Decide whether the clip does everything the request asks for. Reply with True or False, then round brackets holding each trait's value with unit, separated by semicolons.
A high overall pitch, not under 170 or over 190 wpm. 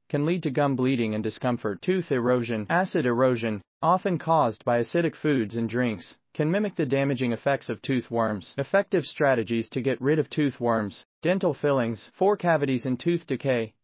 False (135 Hz; 180 wpm)